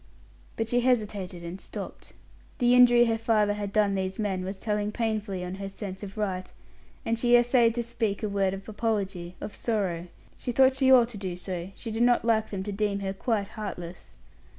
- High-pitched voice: Yes, high, 210 Hz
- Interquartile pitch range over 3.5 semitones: No, average, 3.2 semitones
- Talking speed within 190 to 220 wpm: Yes, average, 200 wpm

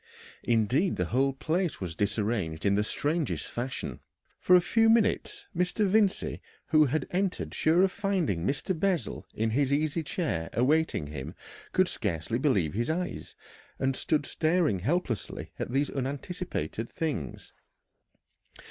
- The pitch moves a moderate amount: No, wide, 8.2 semitones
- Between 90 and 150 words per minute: Yes, average, 140 wpm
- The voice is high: No, medium, 145 Hz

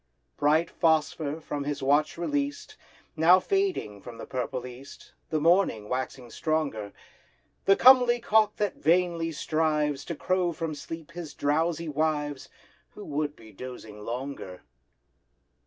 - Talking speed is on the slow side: Yes, slow, 130 wpm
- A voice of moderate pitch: Yes, medium, 155 Hz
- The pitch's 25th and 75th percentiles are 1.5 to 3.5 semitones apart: No, average, 4.1 semitones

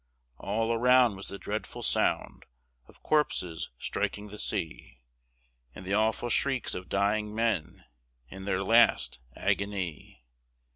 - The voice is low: Yes, low, 105 Hz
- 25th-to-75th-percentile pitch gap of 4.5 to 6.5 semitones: No, average, 3.0 semitones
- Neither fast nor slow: No, slow, 125 wpm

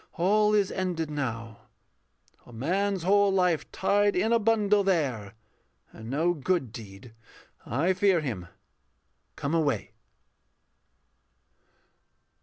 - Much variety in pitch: Yes, wide, 7.5 semitones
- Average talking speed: No, slow, 105 wpm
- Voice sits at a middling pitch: Yes, medium, 175 Hz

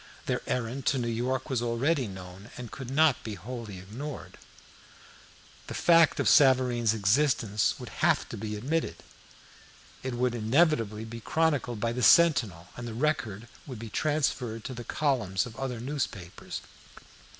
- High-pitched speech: No, low, 120 Hz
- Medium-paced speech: Yes, average, 150 wpm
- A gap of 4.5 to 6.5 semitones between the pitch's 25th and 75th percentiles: No, average, 3.8 semitones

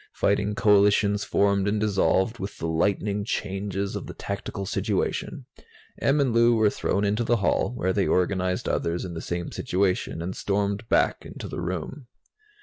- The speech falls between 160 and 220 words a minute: Yes, average, 165 wpm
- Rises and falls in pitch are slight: Yes, narrow, 2.0 semitones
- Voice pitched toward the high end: No, low, 100 Hz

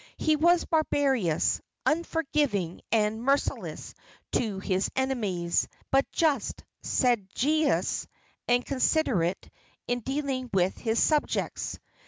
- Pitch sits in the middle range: No, very high, 255 Hz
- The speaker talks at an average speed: No, slow, 95 wpm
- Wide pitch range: Yes, wide, 6.2 semitones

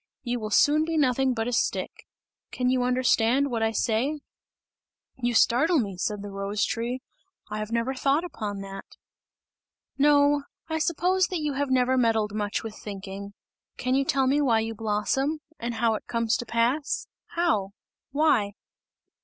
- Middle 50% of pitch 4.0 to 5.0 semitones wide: Yes, average, 4.5 semitones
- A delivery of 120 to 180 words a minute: Yes, average, 165 wpm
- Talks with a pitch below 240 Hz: No, high, 245 Hz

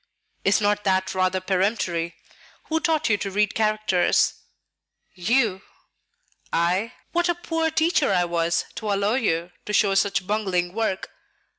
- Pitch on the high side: Yes, high, 200 Hz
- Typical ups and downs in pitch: Yes, average, 3.5 semitones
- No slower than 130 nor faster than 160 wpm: Yes, average, 140 wpm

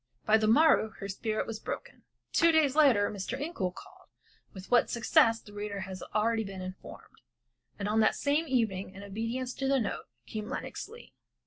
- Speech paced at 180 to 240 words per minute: Yes, average, 185 wpm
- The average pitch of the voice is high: Yes, high, 220 Hz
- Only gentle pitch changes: No, average, 4.4 semitones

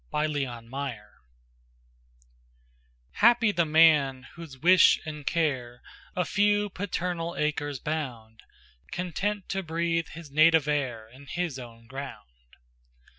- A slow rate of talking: Yes, slow, 115 wpm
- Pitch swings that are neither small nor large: Yes, average, 4.3 semitones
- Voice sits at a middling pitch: Yes, medium, 150 Hz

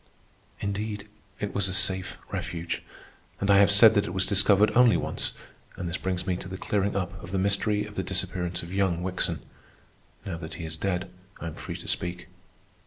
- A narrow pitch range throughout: Yes, narrow, 2.1 semitones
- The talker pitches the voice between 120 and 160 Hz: No, very low, 95 Hz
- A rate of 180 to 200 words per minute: Yes, average, 195 wpm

